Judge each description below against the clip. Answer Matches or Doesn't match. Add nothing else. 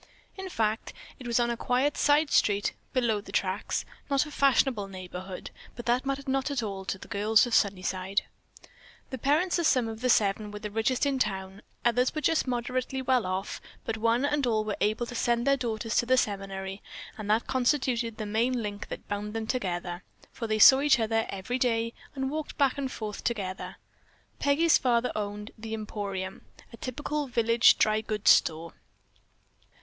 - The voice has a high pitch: Matches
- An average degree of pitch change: Matches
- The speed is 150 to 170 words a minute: Doesn't match